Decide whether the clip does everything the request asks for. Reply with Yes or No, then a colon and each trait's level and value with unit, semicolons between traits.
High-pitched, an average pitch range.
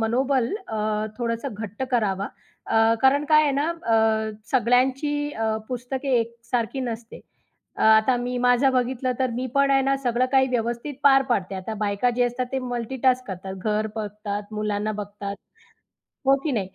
Yes: high, 240 Hz; average, 3.4 semitones